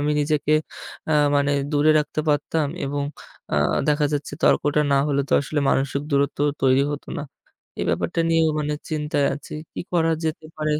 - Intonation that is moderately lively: No, narrow, 1.4 semitones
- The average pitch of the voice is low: No, medium, 145 Hz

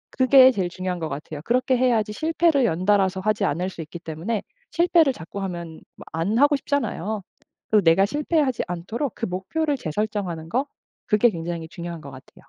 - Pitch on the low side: No, high, 200 Hz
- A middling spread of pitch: No, wide, 7.1 semitones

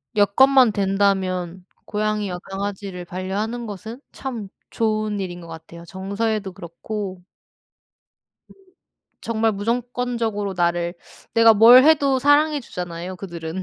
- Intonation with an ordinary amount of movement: Yes, average, 3.7 semitones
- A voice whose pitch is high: Yes, high, 205 Hz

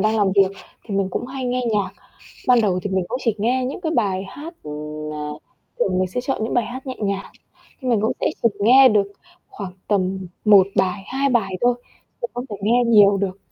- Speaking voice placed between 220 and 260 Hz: No, high, 210 Hz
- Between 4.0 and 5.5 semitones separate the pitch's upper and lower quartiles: Yes, average, 4.3 semitones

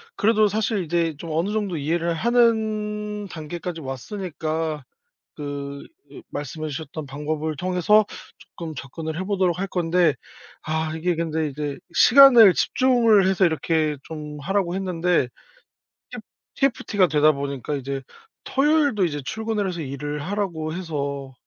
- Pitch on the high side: No, medium, 165 Hz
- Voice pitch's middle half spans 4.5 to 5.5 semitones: Yes, average, 5.2 semitones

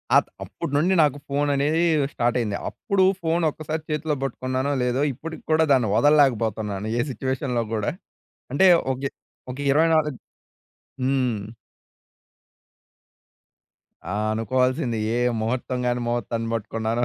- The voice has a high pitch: No, low, 130 Hz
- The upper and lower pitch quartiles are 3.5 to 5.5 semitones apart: Yes, average, 4.0 semitones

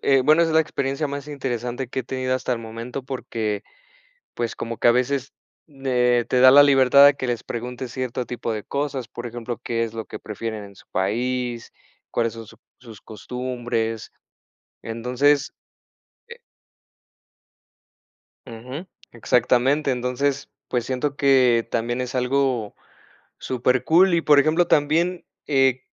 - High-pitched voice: No, low, 125 Hz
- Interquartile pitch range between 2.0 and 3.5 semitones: Yes, average, 2.8 semitones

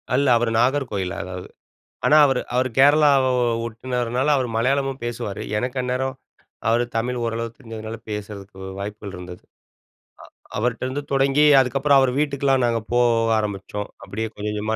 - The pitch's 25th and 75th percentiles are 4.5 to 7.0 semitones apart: No, average, 3.7 semitones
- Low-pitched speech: Yes, low, 120 Hz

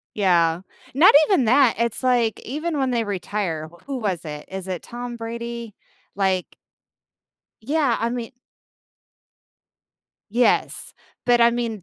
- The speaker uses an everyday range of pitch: Yes, average, 4.3 semitones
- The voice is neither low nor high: No, high, 235 Hz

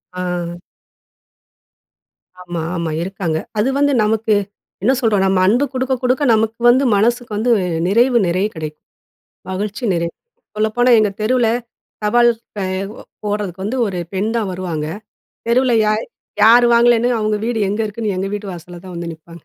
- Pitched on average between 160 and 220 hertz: Yes, high, 215 Hz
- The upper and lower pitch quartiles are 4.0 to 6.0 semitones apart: Yes, average, 4.3 semitones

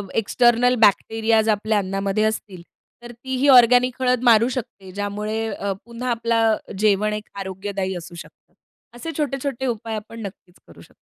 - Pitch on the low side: No, high, 220 Hz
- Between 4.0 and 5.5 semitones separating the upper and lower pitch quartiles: No, average, 3.1 semitones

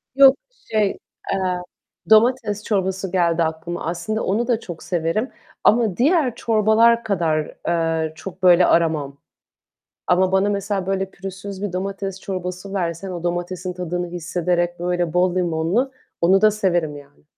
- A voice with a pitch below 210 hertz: Yes, medium, 185 Hz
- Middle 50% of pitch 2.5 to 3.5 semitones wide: Yes, average, 2.8 semitones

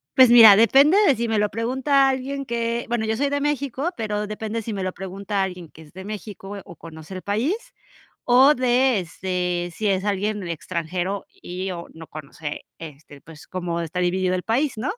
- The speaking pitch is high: Yes, high, 205 Hz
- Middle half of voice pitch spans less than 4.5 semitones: No, average, 4.9 semitones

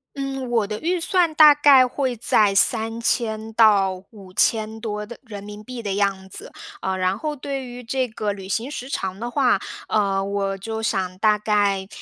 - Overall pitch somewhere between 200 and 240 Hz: Yes, high, 220 Hz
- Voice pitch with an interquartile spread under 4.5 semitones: Yes, average, 4.1 semitones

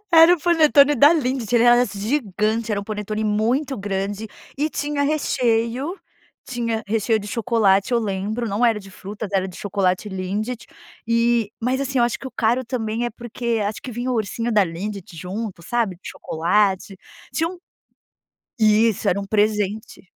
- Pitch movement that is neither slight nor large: Yes, average, 3.2 semitones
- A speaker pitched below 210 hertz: No, high, 220 Hz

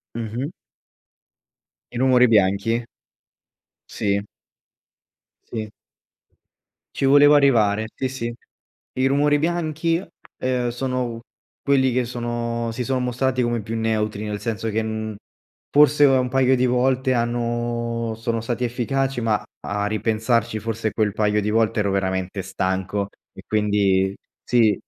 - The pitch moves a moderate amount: Yes, average, 3.0 semitones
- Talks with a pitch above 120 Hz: No, low, 115 Hz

